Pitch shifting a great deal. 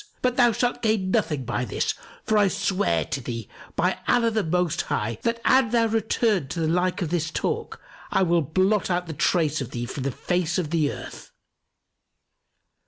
Yes: wide, 6.4 semitones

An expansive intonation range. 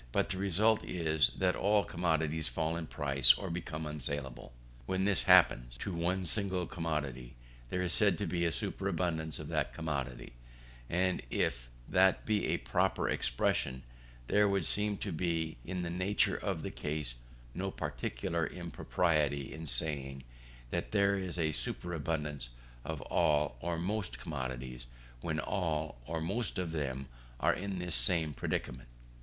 No: average, 4.5 semitones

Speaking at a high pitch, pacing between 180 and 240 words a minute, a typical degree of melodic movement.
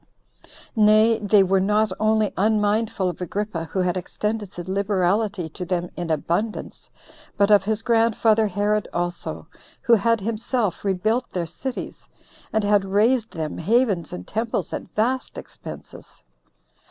No: high, 210 Hz; average, 140 wpm; average, 3.1 semitones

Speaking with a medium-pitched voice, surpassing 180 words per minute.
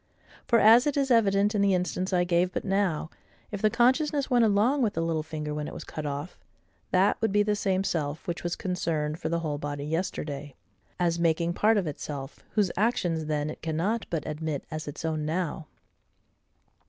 Yes: medium, 175 Hz; average, 200 wpm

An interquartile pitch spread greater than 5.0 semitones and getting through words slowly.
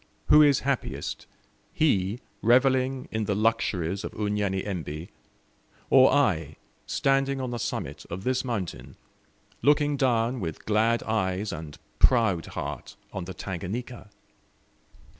Yes: wide, 5.5 semitones; slow, 120 wpm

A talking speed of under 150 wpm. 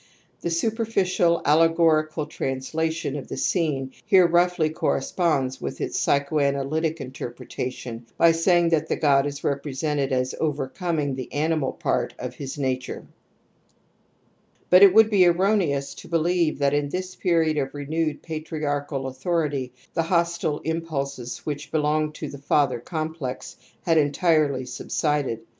Yes: slow, 135 wpm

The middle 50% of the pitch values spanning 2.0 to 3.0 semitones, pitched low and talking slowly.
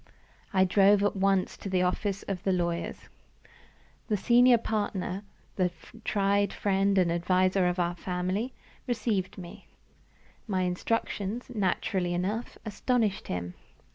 No: narrow, 2.4 semitones; high, 195 Hz; slow, 125 wpm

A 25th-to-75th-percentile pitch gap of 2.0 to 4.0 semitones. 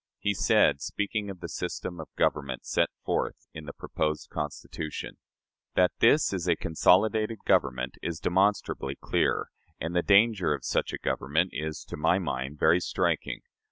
No: average, 4.7 semitones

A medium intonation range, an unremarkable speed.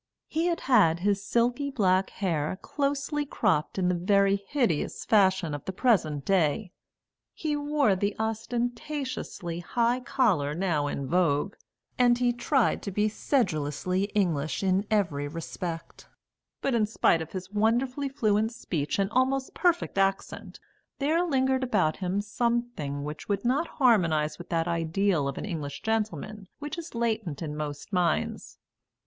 No: wide, 6.5 semitones; average, 145 wpm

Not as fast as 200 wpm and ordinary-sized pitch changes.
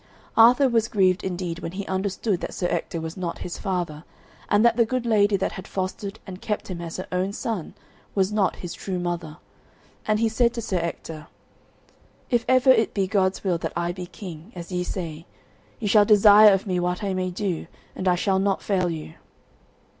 No: fast, 205 wpm; average, 3.1 semitones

